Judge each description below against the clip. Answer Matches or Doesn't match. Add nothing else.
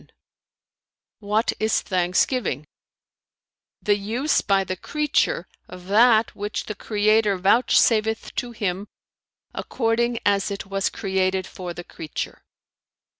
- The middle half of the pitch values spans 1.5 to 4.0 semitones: Matches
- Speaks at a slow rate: Matches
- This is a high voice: Matches